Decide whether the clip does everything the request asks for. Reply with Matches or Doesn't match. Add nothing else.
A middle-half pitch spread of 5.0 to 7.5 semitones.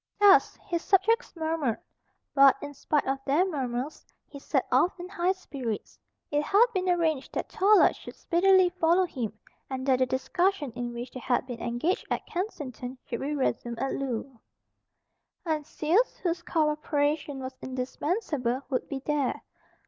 Matches